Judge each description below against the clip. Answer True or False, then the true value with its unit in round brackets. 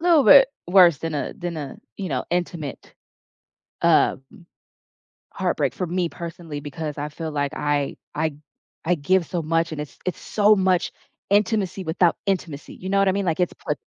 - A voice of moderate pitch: True (170 Hz)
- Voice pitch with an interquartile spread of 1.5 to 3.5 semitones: False (3.9 semitones)